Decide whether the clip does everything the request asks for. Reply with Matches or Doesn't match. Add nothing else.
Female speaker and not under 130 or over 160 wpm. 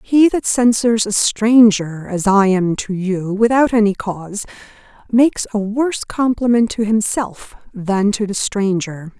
Matches